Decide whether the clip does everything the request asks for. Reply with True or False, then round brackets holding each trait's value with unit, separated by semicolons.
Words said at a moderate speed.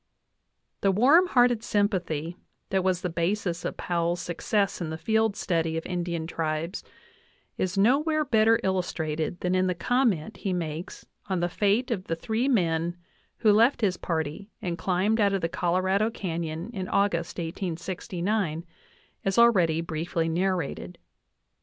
True (145 wpm)